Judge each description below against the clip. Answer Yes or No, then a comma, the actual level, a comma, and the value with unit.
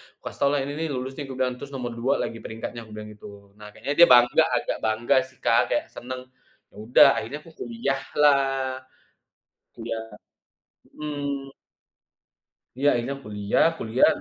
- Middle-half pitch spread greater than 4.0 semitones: No, average, 3.2 semitones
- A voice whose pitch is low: Yes, low, 130 Hz